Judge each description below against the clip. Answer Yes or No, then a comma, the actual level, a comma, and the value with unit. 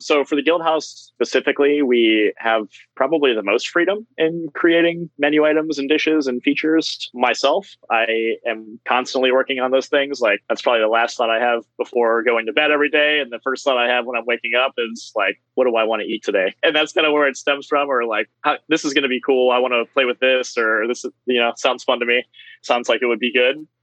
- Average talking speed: No, fast, 245 wpm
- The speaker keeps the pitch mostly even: No, average, 4.0 semitones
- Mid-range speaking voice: No, low, 130 Hz